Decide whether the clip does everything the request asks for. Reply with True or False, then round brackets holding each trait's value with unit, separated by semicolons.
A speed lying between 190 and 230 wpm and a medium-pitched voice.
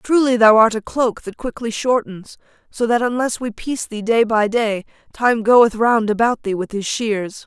False (200 wpm; 225 Hz)